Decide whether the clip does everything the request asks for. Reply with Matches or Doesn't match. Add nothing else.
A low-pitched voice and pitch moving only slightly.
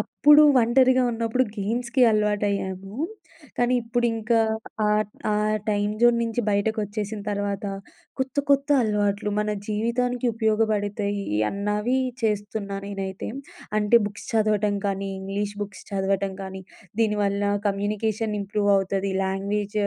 Doesn't match